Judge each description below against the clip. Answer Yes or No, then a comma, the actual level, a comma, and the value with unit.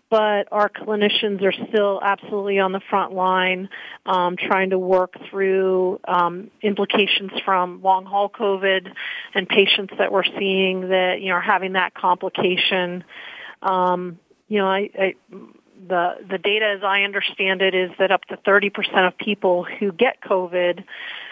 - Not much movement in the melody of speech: Yes, narrow, 1.5 semitones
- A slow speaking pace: No, average, 160 wpm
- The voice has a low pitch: No, high, 190 Hz